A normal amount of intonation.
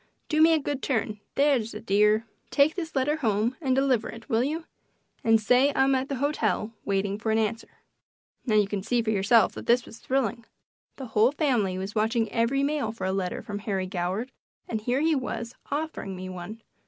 Yes: average, 4.4 semitones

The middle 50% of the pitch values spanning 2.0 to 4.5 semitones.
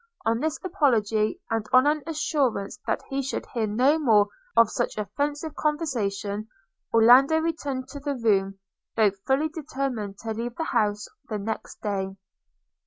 No: wide, 5.4 semitones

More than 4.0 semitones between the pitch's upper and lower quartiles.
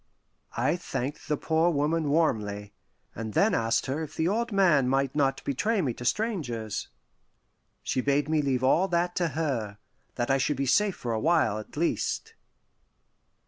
Yes: wide, 5.4 semitones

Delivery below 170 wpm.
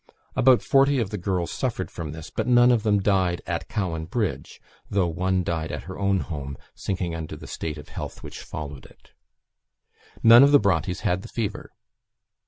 No: average, 190 wpm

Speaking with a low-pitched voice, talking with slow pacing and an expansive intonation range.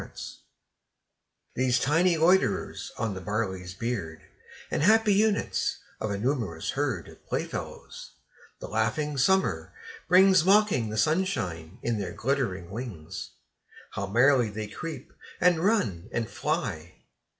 Yes: low, 120 Hz; slow, 125 wpm; wide, 8.9 semitones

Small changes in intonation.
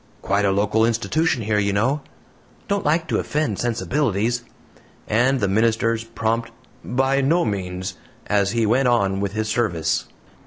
No: average, 3.9 semitones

